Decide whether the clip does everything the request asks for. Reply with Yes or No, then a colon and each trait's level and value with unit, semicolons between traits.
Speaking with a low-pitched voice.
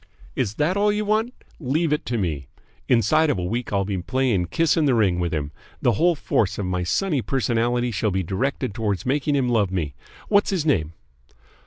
Yes: low, 120 Hz